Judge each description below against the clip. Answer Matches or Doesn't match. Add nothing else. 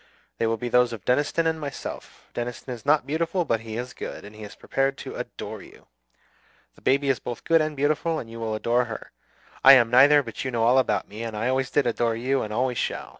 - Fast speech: Matches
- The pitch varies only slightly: Doesn't match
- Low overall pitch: Matches